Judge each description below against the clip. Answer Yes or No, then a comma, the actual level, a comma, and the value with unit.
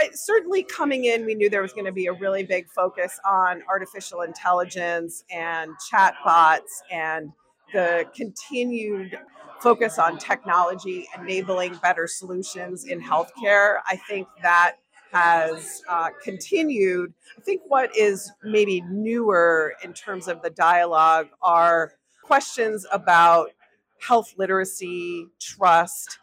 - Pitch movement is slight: No, average, 3.6 semitones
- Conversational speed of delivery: No, slow, 120 wpm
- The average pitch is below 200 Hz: Yes, medium, 185 Hz